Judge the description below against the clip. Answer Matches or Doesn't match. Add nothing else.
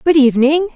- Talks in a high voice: Matches